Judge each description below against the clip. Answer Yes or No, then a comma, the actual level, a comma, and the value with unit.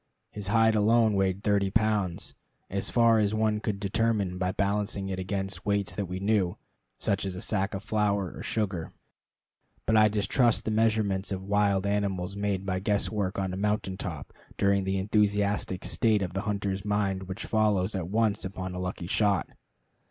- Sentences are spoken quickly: No, average, 175 wpm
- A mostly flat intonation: Yes, narrow, 1.9 semitones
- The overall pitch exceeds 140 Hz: No, low, 100 Hz